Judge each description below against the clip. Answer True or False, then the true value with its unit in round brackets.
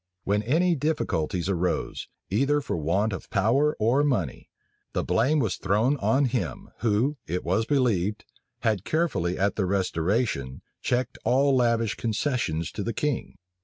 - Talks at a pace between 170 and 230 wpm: False (150 wpm)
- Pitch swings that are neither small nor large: False (6.1 semitones)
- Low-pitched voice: True (110 Hz)